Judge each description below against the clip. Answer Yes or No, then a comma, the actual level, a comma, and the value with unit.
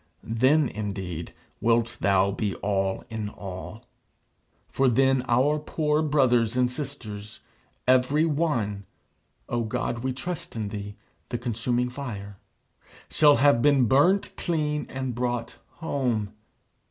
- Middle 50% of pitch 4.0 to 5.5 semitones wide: Yes, average, 5.0 semitones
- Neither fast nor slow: No, slow, 120 wpm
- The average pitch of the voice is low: Yes, low, 125 Hz